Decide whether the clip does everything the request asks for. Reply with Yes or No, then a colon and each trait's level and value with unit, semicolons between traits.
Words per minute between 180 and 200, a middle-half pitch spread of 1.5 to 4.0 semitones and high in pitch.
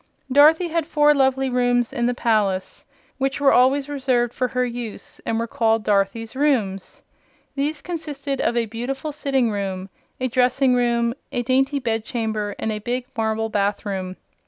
No: average, 160 wpm; average, 3.5 semitones; high, 245 Hz